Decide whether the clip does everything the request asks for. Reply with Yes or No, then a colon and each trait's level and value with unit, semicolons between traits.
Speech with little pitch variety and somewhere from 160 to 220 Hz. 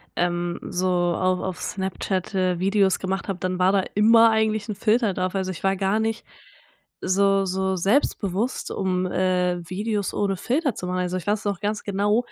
Yes: narrow, 2.1 semitones; high, 190 Hz